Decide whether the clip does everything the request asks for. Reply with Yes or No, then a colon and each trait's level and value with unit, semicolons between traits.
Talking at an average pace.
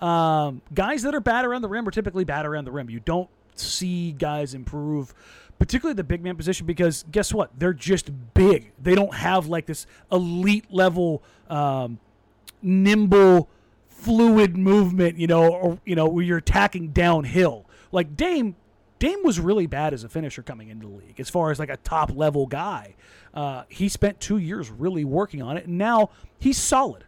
Yes: average, 185 wpm